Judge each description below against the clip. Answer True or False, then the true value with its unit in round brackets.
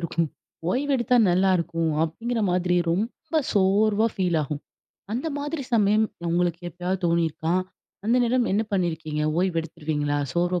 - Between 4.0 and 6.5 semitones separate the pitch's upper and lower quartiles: True (4.7 semitones)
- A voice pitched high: False (180 Hz)